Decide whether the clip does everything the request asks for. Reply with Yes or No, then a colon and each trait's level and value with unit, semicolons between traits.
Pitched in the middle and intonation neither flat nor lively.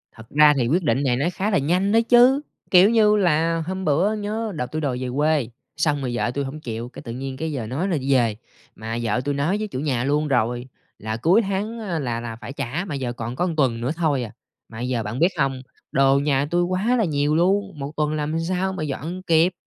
No: medium, 150 Hz; wide, 6.1 semitones